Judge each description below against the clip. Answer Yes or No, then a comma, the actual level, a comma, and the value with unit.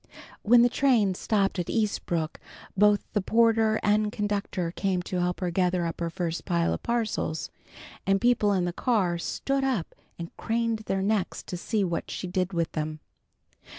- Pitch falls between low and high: No, high, 195 Hz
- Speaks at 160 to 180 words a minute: Yes, average, 175 wpm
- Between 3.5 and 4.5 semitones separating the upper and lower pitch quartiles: Yes, average, 3.8 semitones